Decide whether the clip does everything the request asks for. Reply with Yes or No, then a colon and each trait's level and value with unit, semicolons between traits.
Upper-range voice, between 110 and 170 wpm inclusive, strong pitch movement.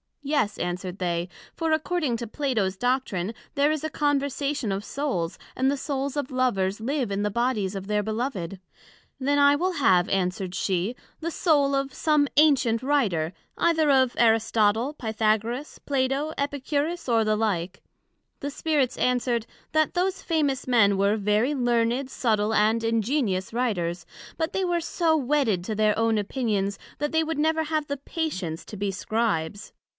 Yes: high, 245 Hz; average, 160 wpm; wide, 5.7 semitones